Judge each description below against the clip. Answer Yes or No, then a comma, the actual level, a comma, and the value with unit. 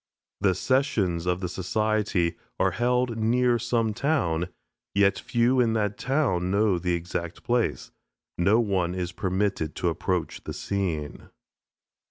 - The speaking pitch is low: Yes, low, 100 Hz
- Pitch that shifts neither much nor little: Yes, average, 4.8 semitones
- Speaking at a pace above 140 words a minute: No, slow, 135 wpm